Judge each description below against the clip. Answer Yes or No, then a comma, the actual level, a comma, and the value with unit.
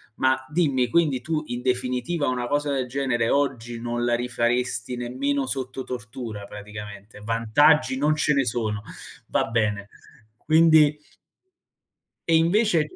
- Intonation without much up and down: No, average, 3.7 semitones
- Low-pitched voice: Yes, low, 125 Hz